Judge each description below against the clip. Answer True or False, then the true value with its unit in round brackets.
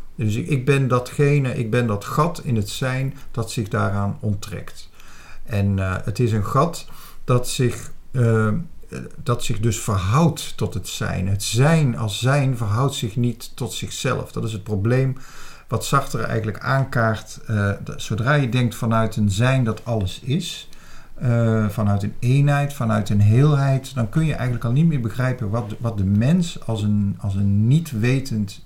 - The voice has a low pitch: True (120 Hz)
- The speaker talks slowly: False (175 wpm)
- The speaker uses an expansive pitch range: False (3.9 semitones)